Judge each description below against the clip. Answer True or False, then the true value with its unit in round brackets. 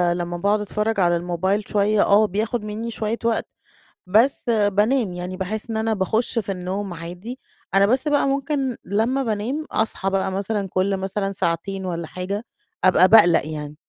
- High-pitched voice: True (205 Hz)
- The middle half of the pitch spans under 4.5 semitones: True (3.1 semitones)